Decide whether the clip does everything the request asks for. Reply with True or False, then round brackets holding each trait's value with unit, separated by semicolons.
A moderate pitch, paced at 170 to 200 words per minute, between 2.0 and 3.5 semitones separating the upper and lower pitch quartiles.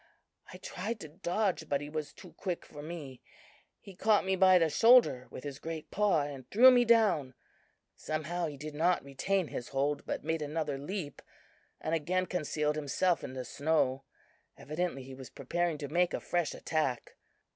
False (155 Hz; 180 wpm; 4.2 semitones)